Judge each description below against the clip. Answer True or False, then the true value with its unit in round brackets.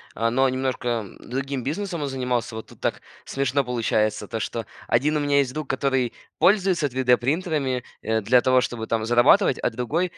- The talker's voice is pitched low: True (130 Hz)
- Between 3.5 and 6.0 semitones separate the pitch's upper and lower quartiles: False (3.0 semitones)